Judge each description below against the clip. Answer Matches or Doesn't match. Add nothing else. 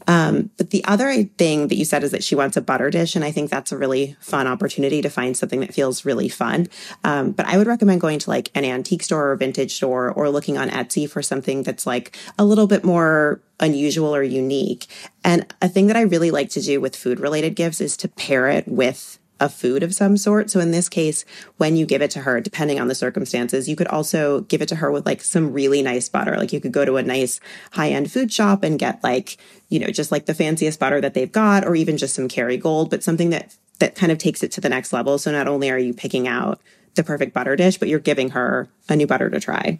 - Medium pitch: Matches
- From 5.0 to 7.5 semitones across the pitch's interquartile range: Matches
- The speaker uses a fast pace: Matches